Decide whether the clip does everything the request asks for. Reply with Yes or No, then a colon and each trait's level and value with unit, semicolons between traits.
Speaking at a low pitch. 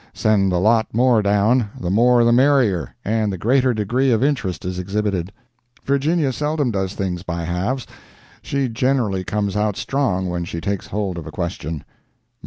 Yes: low, 105 Hz